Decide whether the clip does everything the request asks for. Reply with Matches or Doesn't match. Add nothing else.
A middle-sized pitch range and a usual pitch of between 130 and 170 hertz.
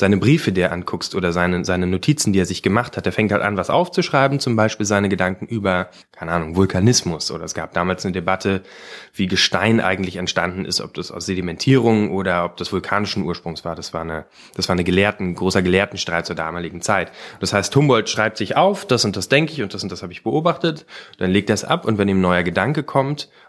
Doesn't match